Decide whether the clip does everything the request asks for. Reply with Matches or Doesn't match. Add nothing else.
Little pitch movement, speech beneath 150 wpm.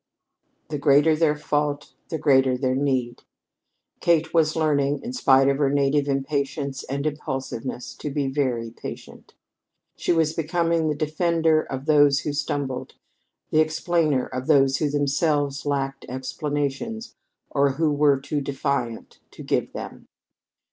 Matches